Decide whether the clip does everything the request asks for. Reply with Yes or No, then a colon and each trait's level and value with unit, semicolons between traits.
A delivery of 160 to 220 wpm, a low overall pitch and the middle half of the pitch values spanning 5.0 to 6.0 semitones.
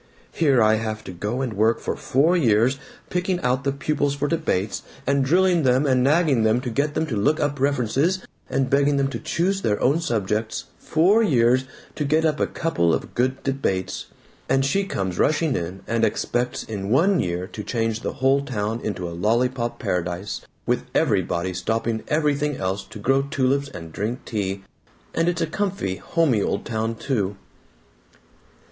Yes: average, 180 wpm; low, 130 Hz; wide, 5.4 semitones